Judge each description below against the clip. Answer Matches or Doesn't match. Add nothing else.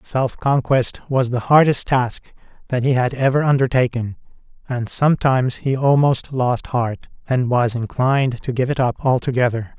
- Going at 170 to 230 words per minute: Doesn't match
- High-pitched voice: Doesn't match